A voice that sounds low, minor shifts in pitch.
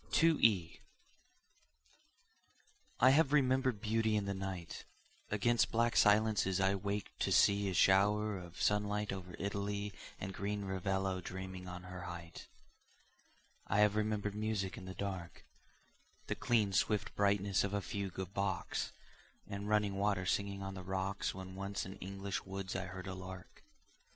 Yes: low, 100 Hz; narrow, 1.7 semitones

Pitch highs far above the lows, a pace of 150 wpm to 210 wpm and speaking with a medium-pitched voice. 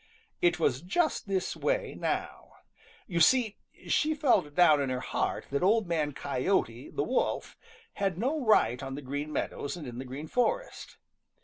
Yes: wide, 8.4 semitones; average, 170 wpm; medium, 170 Hz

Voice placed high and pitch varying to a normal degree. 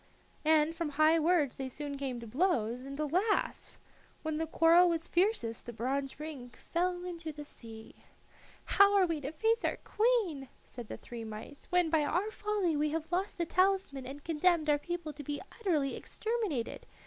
Yes: very high, 315 Hz; average, 4.4 semitones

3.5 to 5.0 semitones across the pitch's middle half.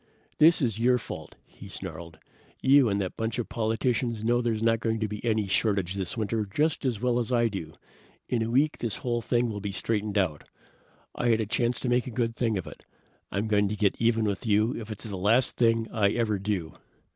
No: narrow, 2.6 semitones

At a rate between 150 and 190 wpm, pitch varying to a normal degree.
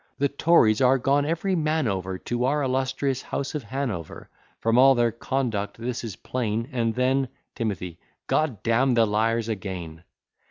Yes: average, 170 wpm; average, 3.7 semitones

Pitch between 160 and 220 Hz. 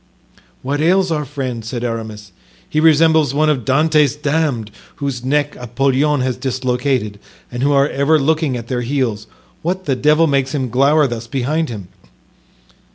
No: low, 135 Hz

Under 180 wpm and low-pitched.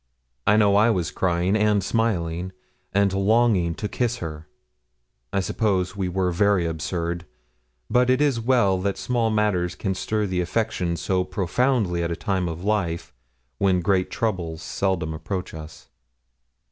Yes: average, 150 wpm; very low, 95 Hz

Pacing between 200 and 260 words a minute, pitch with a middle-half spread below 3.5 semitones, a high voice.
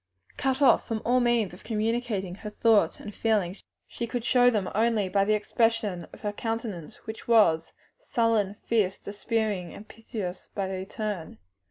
No: average, 160 wpm; average, 2.7 semitones; high, 215 Hz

